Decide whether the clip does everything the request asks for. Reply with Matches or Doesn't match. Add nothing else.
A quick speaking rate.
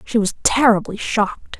Doesn't match